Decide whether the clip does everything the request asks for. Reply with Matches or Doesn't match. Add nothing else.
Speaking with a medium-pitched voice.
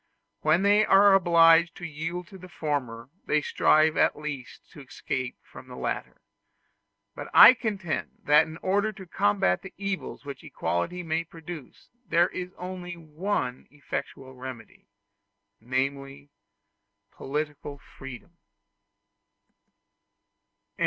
Matches